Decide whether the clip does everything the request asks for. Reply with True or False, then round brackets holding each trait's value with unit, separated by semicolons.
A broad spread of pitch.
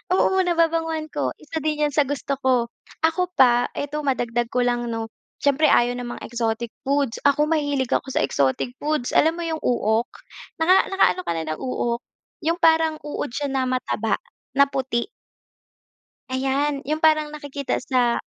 False (4.2 semitones)